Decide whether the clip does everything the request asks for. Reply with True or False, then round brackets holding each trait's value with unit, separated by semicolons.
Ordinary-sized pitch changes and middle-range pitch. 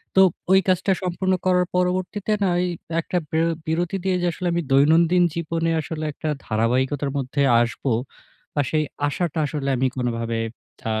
True (4.6 semitones; 165 Hz)